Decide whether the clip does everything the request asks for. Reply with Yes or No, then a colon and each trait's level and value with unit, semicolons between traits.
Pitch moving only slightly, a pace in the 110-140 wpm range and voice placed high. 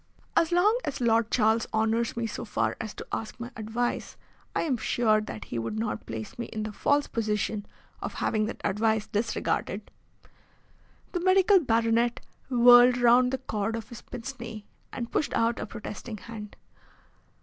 No: narrow, 2.2 semitones; average, 170 wpm; high, 230 Hz